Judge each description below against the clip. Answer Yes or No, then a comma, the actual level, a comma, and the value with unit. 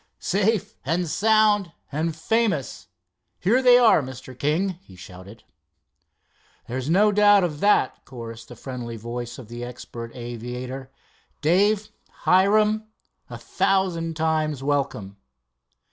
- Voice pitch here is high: No, medium, 155 Hz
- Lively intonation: Yes, wide, 8.3 semitones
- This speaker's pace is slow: Yes, slow, 115 wpm